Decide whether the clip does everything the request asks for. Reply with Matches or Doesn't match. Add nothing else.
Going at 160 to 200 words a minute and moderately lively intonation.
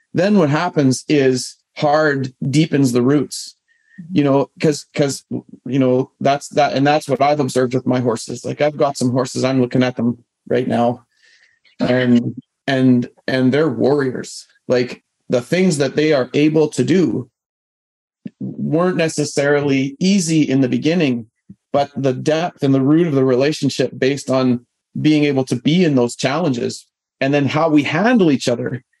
Matches